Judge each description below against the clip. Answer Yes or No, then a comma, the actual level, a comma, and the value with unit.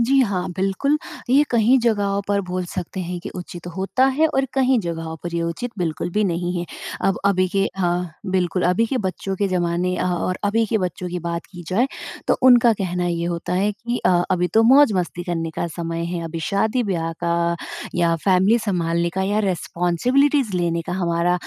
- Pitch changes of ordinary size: Yes, average, 3.7 semitones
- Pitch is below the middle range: No, medium, 185 Hz